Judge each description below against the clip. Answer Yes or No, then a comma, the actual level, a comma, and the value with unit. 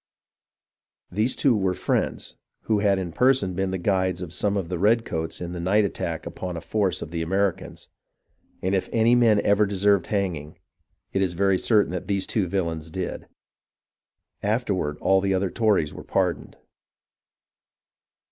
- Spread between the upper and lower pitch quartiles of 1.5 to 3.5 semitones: Yes, narrow, 2.6 semitones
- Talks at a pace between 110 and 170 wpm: Yes, average, 160 wpm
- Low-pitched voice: Yes, very low, 95 Hz